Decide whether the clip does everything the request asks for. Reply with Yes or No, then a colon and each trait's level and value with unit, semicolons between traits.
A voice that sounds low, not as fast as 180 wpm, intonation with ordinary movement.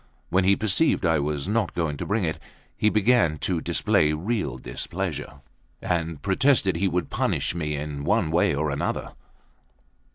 Yes: very low, 85 Hz; average, 160 wpm; average, 4.5 semitones